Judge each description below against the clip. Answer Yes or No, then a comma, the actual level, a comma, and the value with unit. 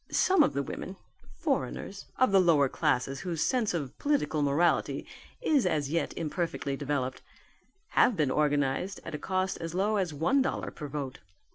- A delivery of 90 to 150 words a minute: No, average, 165 wpm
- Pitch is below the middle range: No, medium, 165 Hz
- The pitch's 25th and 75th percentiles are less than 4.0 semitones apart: No, average, 5.3 semitones